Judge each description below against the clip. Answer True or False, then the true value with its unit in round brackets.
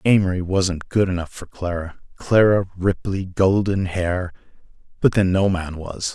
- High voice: False (95 Hz)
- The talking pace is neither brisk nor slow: True (155 wpm)